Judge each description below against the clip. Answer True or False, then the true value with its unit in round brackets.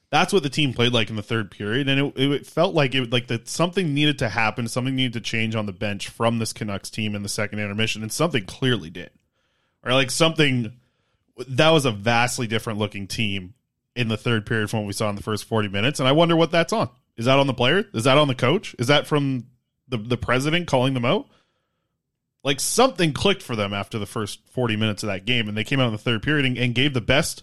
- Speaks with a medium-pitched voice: False (125 Hz)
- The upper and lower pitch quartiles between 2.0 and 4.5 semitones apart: True (4.1 semitones)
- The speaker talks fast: True (250 wpm)